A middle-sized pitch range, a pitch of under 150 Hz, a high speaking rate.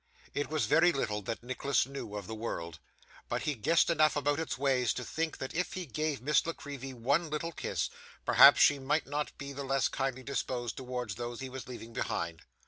Yes: average, 3.7 semitones; low, 135 Hz; fast, 210 wpm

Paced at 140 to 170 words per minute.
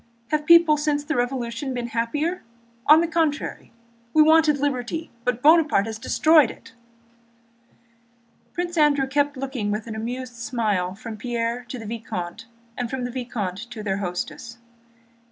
Yes: average, 150 wpm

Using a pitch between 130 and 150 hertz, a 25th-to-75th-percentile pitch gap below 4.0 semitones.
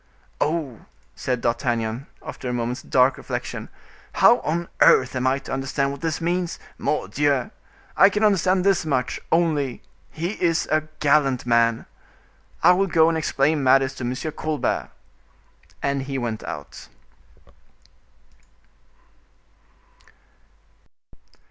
No: medium, 140 Hz; average, 4.3 semitones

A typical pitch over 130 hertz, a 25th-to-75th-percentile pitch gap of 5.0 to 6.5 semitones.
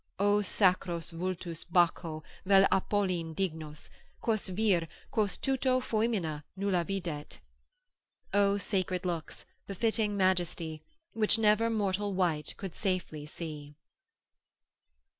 No: medium, 185 Hz; average, 3.5 semitones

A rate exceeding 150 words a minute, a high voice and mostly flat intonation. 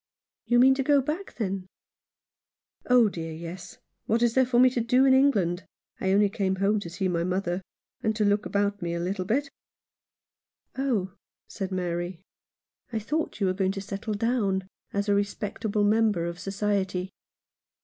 No: average, 180 wpm; high, 200 Hz; average, 3.8 semitones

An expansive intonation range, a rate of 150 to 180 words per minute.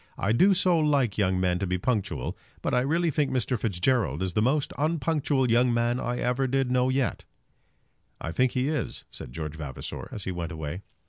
No: wide, 6.6 semitones; average, 200 wpm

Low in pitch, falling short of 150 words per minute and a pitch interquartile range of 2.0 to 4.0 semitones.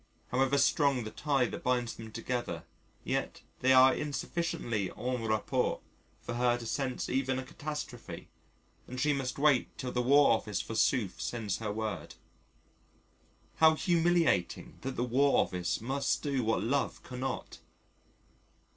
Yes: low, 125 Hz; average, 140 wpm; average, 3.5 semitones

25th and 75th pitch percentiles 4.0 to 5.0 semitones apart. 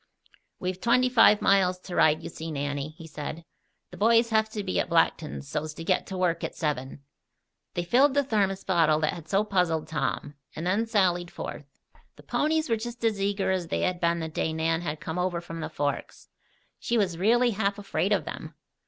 Yes: average, 4.7 semitones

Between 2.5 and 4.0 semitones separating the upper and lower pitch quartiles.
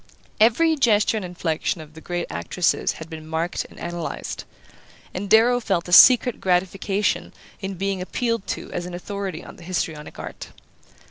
Yes: average, 3.6 semitones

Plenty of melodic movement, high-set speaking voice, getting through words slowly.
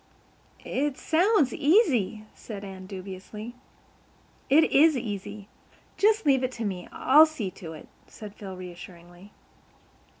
Yes: wide, 7.3 semitones; high, 215 Hz; slow, 125 wpm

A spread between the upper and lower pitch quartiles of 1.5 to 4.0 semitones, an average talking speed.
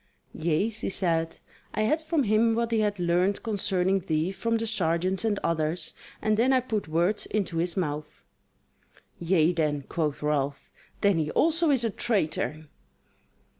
No: average, 5.3 semitones; average, 160 wpm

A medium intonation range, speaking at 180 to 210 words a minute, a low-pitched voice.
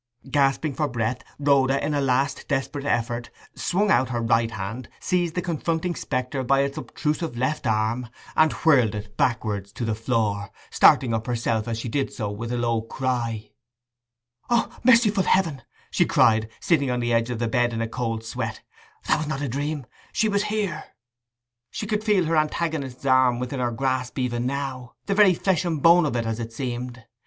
Yes: average, 4.8 semitones; average, 185 wpm; low, 130 Hz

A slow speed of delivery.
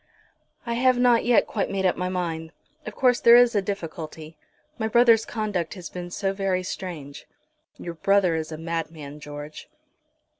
No: average, 165 wpm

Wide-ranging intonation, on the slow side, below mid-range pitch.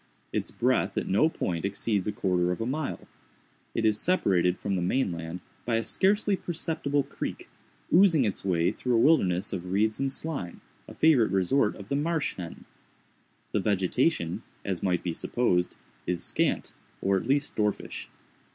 No: wide, 7.5 semitones; average, 170 wpm; low, 105 Hz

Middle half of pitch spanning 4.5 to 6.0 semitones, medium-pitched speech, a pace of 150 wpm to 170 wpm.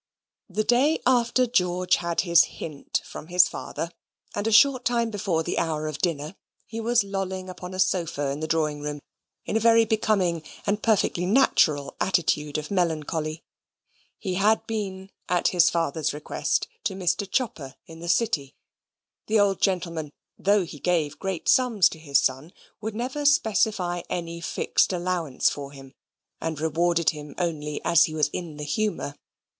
Yes: average, 5.0 semitones; medium, 175 Hz; average, 165 wpm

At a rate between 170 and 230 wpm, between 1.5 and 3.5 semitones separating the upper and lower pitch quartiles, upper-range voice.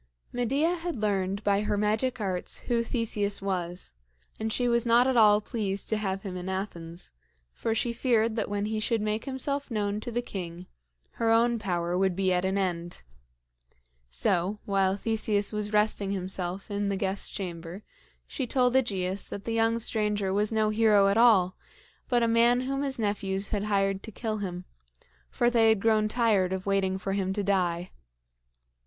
Yes: average, 180 wpm; average, 3.0 semitones; high, 205 Hz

